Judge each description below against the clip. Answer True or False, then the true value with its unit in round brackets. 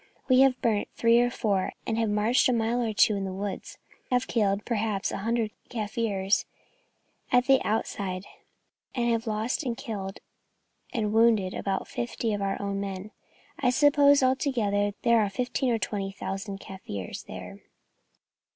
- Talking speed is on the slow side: False (155 wpm)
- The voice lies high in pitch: True (220 Hz)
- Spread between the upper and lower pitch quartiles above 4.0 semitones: False (3.3 semitones)